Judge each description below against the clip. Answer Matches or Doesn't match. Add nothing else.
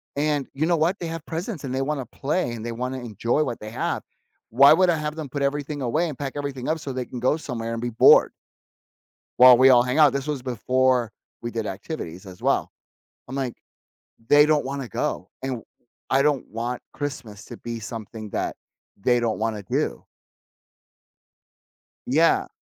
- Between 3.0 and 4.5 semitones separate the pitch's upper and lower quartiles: Matches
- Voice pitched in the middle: Doesn't match